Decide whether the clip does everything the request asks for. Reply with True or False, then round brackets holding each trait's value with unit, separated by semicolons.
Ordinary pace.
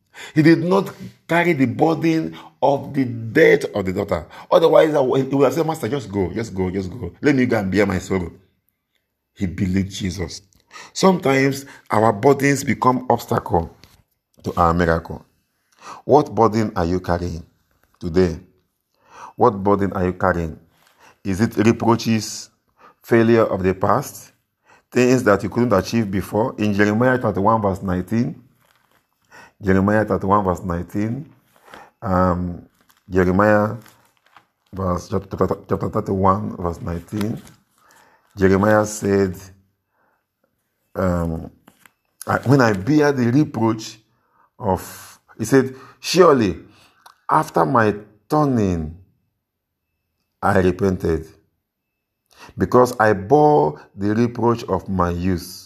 False (115 wpm)